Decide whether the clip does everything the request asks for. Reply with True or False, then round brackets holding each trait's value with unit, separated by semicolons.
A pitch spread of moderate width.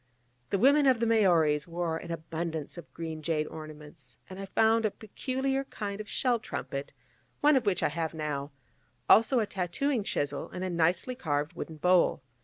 False (6.1 semitones)